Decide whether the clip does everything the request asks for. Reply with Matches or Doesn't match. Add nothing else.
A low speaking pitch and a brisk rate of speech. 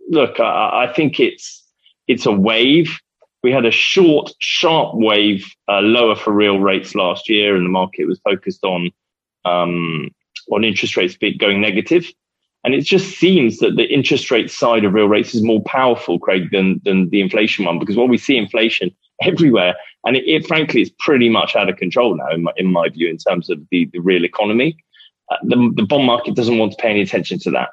Matches